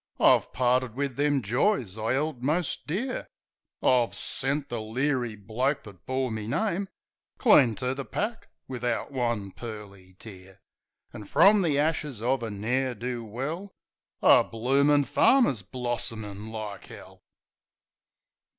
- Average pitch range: Yes, average, 4.6 semitones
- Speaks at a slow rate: Yes, slow, 130 wpm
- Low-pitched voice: Yes, low, 125 Hz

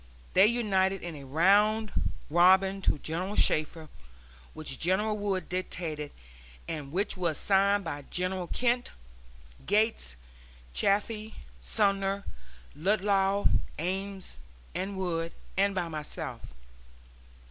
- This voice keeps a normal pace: No, slow, 105 wpm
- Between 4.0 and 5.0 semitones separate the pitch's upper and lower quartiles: No, average, 3.3 semitones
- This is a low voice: No, high, 190 Hz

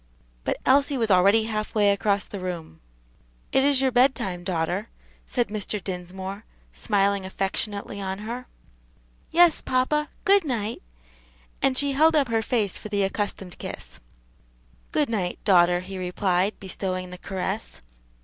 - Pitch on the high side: Yes, high, 205 Hz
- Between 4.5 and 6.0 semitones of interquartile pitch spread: Yes, average, 4.8 semitones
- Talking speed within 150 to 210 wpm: No, average, 140 wpm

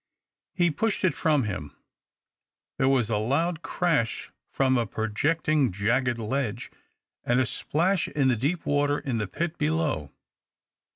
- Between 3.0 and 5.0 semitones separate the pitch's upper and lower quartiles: No, wide, 5.4 semitones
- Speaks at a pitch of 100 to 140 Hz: Yes, low, 135 Hz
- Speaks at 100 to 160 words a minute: Yes, average, 140 wpm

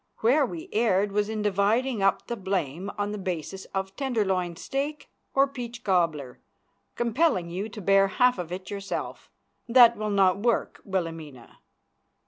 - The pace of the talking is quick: No, average, 150 wpm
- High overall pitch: Yes, high, 200 Hz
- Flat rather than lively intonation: No, average, 4.2 semitones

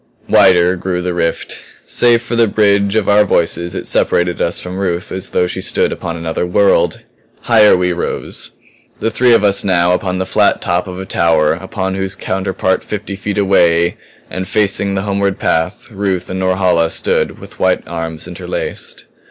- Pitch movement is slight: Yes, narrow, 2.2 semitones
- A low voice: Yes, very low, 95 Hz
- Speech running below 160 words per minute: No, average, 175 wpm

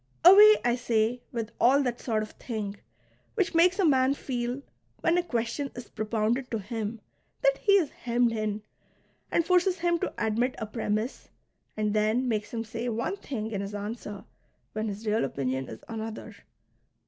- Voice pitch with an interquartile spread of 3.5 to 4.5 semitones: Yes, average, 4.0 semitones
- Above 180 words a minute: No, average, 170 wpm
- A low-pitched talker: No, high, 230 Hz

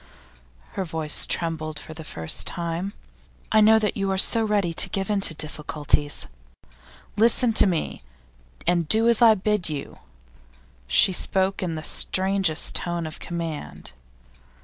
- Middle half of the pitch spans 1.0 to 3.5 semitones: No, average, 4.4 semitones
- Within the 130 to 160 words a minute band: Yes, average, 150 wpm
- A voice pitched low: No, medium, 175 Hz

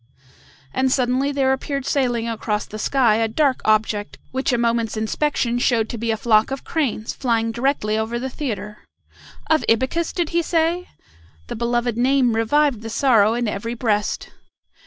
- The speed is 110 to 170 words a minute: Yes, average, 165 wpm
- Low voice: No, high, 240 Hz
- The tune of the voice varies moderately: Yes, average, 3.4 semitones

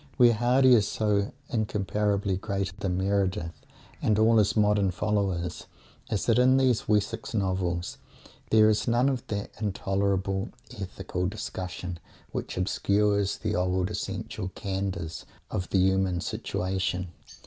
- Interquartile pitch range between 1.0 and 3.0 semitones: Yes, narrow, 2.4 semitones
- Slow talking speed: Yes, slow, 130 wpm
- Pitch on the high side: No, low, 100 Hz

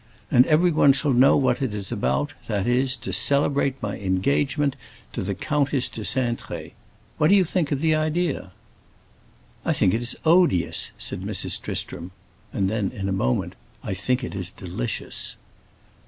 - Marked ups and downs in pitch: Yes, wide, 6.9 semitones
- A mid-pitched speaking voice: No, low, 130 Hz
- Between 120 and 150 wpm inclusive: No, average, 165 wpm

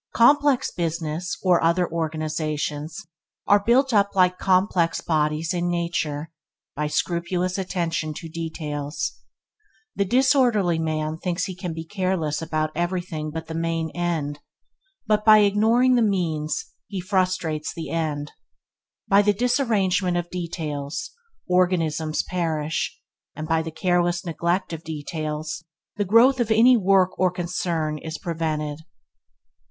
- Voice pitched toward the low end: No, medium, 170 Hz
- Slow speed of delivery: Yes, slow, 130 wpm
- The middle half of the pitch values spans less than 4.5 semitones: Yes, average, 3.3 semitones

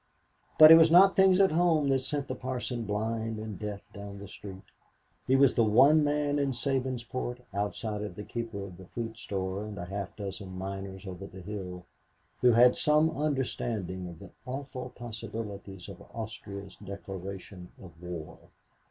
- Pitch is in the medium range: No, low, 110 Hz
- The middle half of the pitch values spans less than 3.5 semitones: No, average, 5.1 semitones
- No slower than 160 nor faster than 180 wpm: Yes, average, 170 wpm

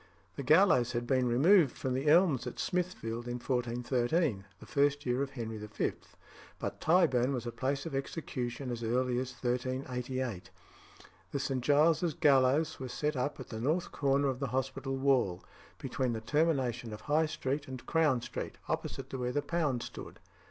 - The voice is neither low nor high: No, low, 130 Hz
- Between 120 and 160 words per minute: No, average, 175 wpm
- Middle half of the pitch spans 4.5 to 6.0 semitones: No, average, 3.0 semitones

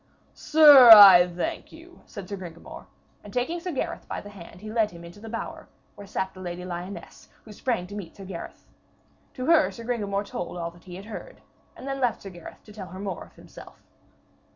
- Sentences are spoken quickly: Yes, fast, 215 wpm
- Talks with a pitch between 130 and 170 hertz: No, high, 200 Hz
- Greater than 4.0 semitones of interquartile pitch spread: Yes, average, 4.6 semitones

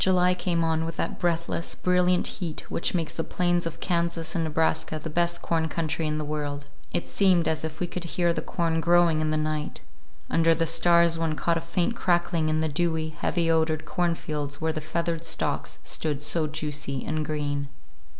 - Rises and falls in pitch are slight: Yes, narrow, 1.8 semitones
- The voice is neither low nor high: Yes, medium, 165 Hz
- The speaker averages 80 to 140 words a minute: No, average, 200 wpm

